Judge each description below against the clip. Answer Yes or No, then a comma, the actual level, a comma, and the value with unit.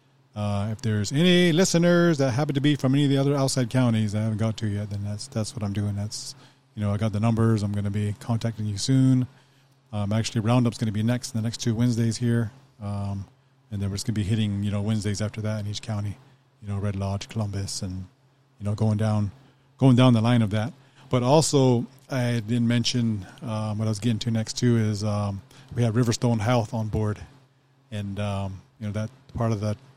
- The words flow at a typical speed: No, fast, 235 wpm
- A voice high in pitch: No, low, 115 Hz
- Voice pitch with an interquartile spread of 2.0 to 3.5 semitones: No, average, 3.9 semitones